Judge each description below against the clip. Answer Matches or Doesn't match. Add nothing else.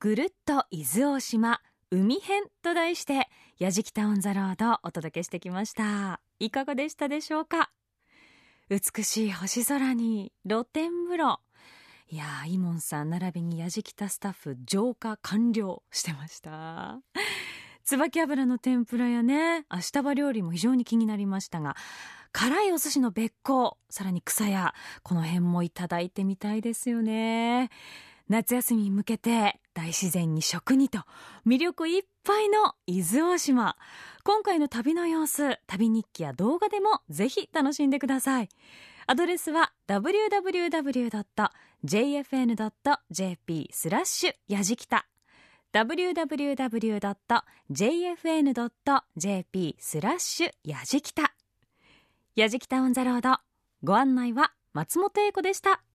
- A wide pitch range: Matches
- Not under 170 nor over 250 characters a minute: Matches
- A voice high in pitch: Matches